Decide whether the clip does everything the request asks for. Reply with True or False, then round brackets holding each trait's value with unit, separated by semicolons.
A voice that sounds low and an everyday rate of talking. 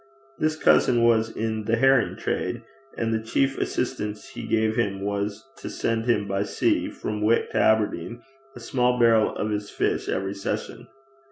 True (110 Hz; 170 wpm)